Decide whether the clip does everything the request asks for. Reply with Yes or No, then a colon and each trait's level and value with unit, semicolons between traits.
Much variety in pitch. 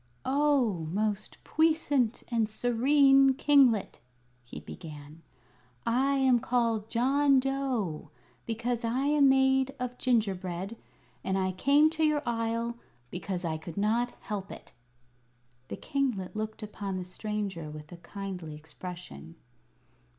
Yes: wide, 6.0 semitones